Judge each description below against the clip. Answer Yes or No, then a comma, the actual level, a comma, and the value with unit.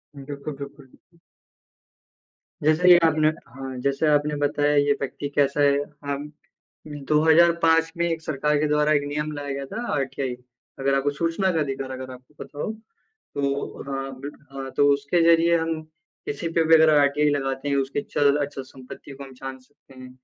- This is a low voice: No, medium, 145 Hz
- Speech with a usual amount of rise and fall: No, narrow, 2.2 semitones